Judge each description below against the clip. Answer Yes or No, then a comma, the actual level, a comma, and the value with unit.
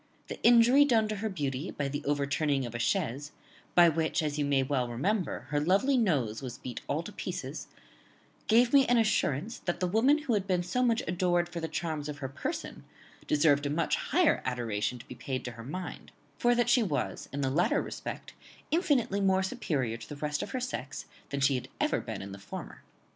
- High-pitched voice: No, medium, 160 Hz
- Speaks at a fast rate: Yes, fast, 210 wpm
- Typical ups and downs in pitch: No, wide, 7.9 semitones